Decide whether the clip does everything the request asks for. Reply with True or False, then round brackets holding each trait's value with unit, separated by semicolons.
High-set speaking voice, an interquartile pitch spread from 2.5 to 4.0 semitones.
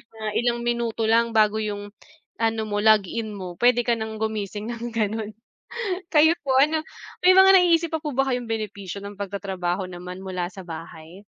True (220 Hz; 3.1 semitones)